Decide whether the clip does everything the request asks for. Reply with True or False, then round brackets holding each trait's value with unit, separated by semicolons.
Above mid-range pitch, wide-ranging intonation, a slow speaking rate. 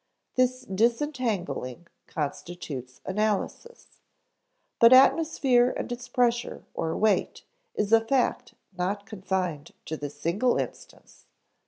True (215 Hz; 6.2 semitones; 105 wpm)